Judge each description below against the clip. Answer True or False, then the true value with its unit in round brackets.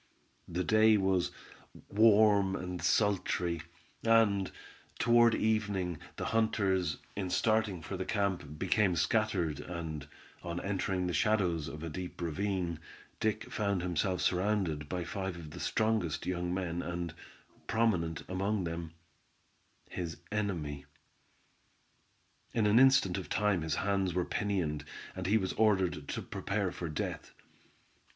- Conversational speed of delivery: False (130 wpm)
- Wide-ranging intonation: False (3.5 semitones)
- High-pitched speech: False (95 Hz)